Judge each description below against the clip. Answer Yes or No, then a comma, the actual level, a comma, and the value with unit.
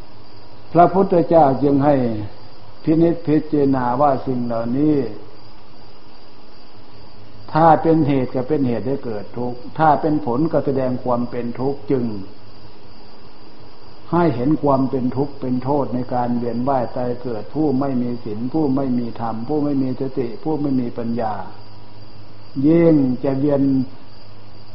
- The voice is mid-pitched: No, low, 125 Hz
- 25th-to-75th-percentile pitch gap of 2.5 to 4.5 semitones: No, average, 4.9 semitones